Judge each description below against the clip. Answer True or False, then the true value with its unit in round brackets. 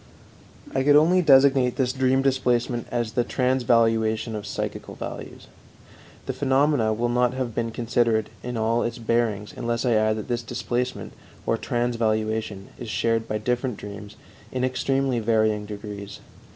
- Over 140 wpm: True (150 wpm)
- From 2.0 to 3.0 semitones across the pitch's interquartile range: True (2.5 semitones)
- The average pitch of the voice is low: True (120 Hz)